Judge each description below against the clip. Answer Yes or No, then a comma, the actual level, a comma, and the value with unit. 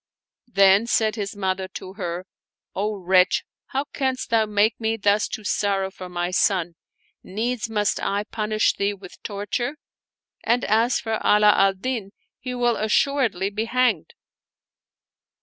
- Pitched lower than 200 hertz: No, high, 210 Hz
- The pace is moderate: Yes, average, 150 wpm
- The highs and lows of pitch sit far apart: No, average, 2.8 semitones